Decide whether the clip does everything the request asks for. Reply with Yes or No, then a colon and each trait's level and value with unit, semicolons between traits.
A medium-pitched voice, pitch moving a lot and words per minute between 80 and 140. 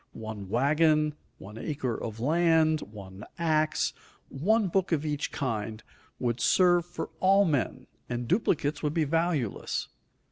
Yes: medium, 150 Hz; wide, 5.9 semitones; slow, 135 wpm